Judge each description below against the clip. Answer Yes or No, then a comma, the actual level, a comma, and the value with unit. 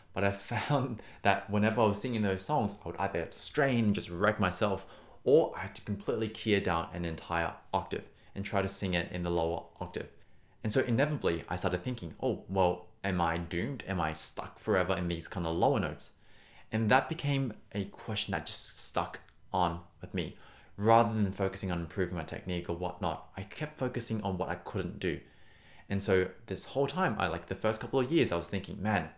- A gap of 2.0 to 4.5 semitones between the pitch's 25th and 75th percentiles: Yes, average, 3.9 semitones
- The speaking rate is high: Yes, fast, 210 wpm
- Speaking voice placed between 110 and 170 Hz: No, low, 100 Hz